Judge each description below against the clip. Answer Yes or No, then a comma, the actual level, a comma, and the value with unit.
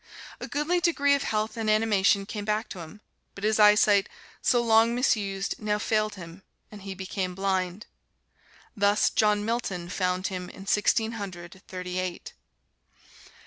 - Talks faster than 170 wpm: No, average, 150 wpm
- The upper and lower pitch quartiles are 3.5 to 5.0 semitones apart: No, narrow, 2.6 semitones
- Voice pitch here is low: No, high, 205 Hz